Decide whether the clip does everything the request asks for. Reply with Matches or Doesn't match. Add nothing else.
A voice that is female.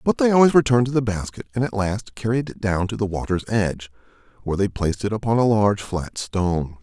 Doesn't match